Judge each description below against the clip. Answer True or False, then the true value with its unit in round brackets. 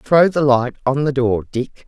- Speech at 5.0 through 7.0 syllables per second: False (4.2 syllables/s)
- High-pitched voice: False (135 Hz)